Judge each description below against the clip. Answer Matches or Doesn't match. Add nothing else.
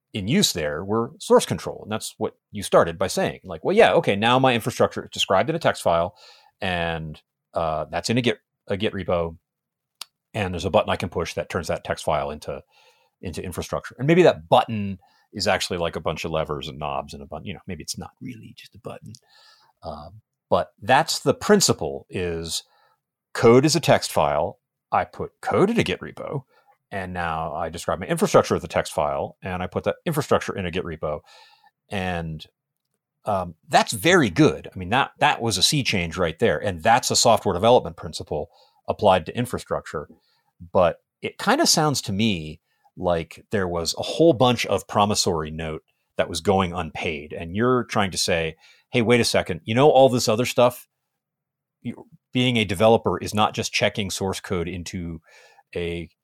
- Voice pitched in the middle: Doesn't match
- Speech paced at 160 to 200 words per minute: Matches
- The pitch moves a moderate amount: Doesn't match